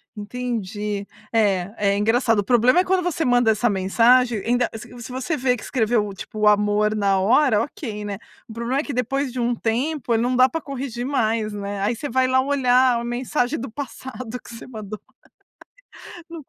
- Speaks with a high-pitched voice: Yes, high, 240 Hz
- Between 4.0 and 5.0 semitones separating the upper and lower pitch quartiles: No, average, 3.4 semitones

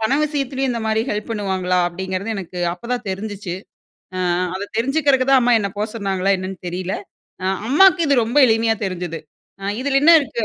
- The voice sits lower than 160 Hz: No, high, 220 Hz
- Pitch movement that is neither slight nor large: No, wide, 5.7 semitones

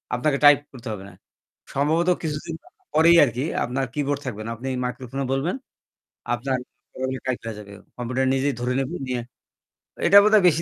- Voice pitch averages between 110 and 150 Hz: Yes, low, 135 Hz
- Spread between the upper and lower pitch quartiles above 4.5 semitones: No, average, 3.2 semitones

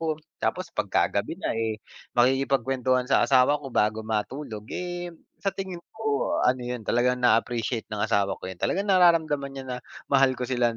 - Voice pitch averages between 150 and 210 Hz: No, low, 130 Hz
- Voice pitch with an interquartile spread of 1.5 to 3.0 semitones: No, average, 4.5 semitones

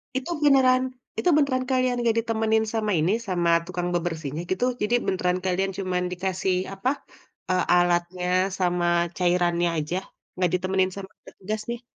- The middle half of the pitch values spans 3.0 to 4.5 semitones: Yes, average, 3.9 semitones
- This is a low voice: No, medium, 185 Hz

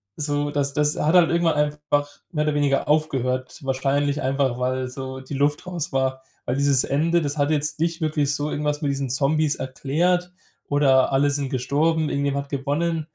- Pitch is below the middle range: No, medium, 145 Hz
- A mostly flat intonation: Yes, narrow, 2.0 semitones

